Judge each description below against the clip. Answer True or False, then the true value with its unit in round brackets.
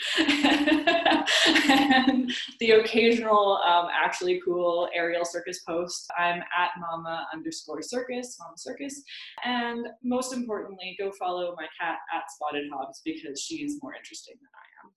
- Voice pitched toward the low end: False (220 Hz)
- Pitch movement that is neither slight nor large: False (7.9 semitones)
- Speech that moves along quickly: False (135 wpm)